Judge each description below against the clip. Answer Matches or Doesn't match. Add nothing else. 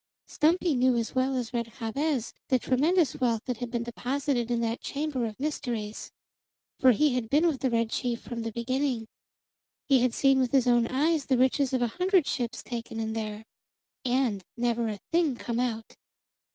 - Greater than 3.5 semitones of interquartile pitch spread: Doesn't match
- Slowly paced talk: Doesn't match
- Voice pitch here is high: Matches